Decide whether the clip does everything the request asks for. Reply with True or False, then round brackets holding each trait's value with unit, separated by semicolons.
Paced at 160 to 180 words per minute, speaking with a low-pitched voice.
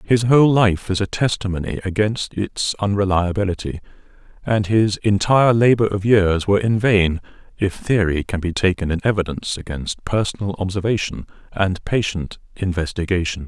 False (140 wpm; 100 Hz)